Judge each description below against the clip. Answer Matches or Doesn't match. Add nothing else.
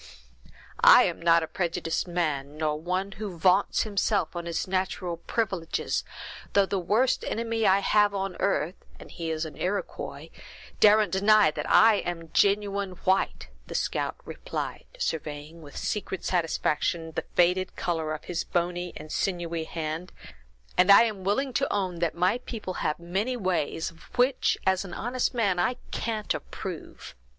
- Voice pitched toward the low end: Doesn't match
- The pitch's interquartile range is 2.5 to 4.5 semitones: Matches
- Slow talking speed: Doesn't match